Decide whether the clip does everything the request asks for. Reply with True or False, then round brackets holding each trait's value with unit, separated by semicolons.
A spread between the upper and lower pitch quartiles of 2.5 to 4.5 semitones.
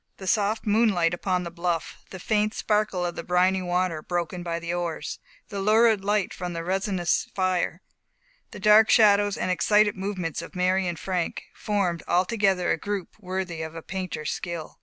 True (2.8 semitones)